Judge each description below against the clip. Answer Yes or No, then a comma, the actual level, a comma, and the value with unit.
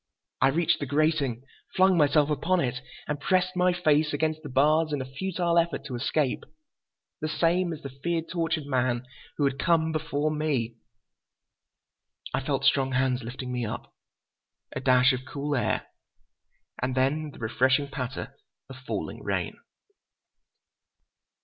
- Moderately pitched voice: Yes, medium, 145 Hz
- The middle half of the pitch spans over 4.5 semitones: No, average, 3.5 semitones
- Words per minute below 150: Yes, slow, 135 wpm